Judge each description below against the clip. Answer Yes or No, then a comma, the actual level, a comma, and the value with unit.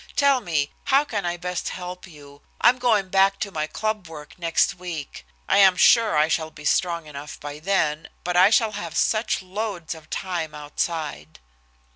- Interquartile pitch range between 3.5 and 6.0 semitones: Yes, average, 4.4 semitones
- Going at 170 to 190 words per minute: Yes, average, 180 wpm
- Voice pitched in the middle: Yes, medium, 175 Hz